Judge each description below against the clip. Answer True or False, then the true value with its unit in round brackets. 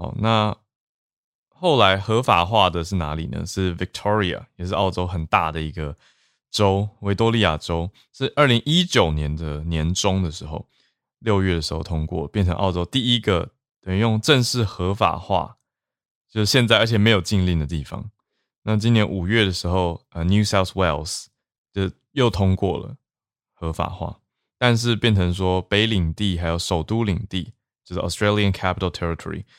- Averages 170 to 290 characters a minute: False (320 characters per minute)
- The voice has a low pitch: True (95 Hz)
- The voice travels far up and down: False (3.9 semitones)